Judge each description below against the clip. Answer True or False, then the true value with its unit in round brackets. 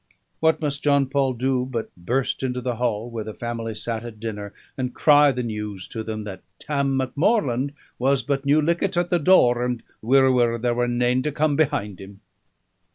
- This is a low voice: True (125 Hz)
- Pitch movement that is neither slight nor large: True (3.6 semitones)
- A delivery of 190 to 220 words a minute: True (195 wpm)